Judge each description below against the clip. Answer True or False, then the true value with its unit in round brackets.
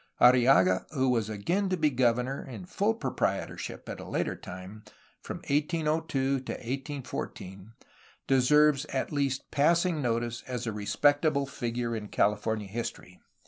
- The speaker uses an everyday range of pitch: True (4.5 semitones)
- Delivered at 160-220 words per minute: False (135 wpm)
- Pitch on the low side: True (130 Hz)